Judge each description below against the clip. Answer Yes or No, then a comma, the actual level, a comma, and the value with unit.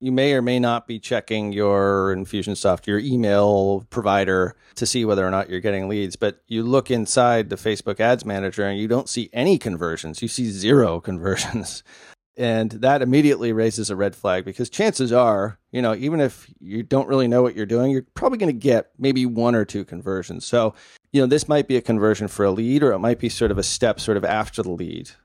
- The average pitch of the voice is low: Yes, low, 110 Hz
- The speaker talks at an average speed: No, fast, 220 wpm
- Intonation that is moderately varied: Yes, average, 3.9 semitones